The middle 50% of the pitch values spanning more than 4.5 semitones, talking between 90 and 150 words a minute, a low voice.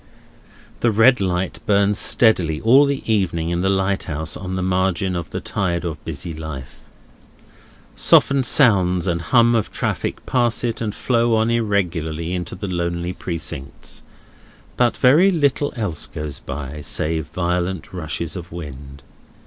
Yes: average, 5.1 semitones; average, 145 wpm; very low, 90 Hz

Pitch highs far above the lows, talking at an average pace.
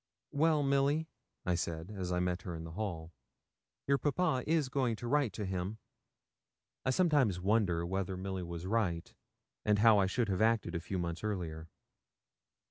Yes: wide, 6.4 semitones; average, 170 wpm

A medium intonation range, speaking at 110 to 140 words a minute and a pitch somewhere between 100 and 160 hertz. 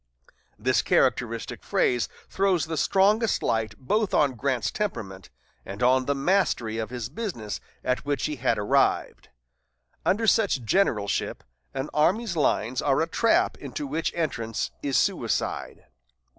No: wide, 8.5 semitones; slow, 135 wpm; medium, 140 Hz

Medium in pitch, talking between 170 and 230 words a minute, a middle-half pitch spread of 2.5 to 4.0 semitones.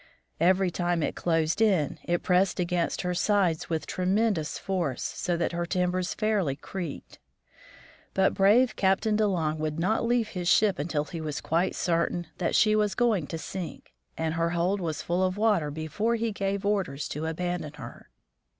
Yes: medium, 180 Hz; average, 175 wpm; average, 3.5 semitones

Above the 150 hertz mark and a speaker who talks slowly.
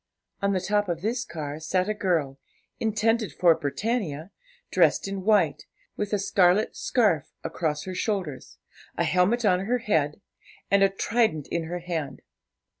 No: medium, 185 Hz; average, 155 wpm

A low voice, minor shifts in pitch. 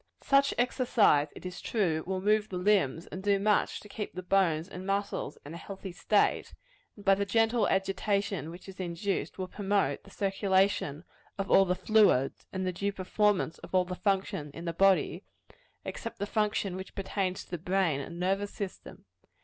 No: high, 195 Hz; narrow, 2.1 semitones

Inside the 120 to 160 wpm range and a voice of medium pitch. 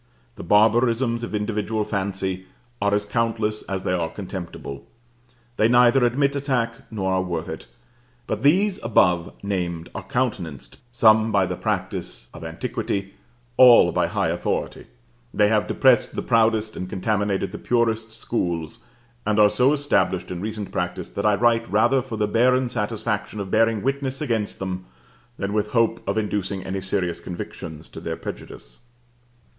No: average, 155 wpm; low, 105 Hz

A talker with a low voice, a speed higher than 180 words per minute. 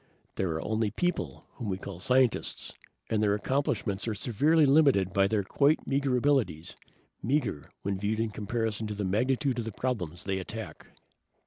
No: low, 110 Hz; average, 165 wpm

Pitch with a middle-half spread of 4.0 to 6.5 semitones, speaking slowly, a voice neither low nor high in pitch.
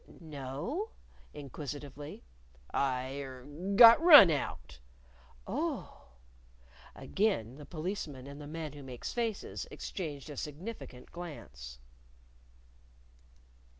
Yes: average, 5.0 semitones; slow, 90 wpm; medium, 145 Hz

